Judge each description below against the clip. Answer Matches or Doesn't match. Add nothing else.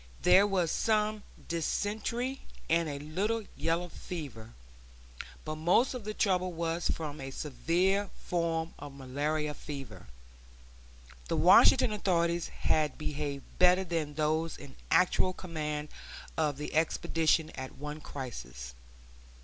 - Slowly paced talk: Matches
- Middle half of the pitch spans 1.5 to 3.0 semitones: Doesn't match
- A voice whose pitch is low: Doesn't match